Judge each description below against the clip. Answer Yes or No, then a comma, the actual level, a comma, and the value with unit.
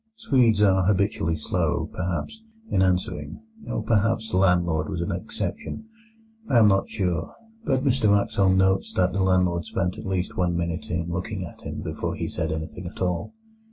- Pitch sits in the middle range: No, very low, 95 Hz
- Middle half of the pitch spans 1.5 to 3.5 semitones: Yes, average, 2.8 semitones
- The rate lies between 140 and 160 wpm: No, average, 175 wpm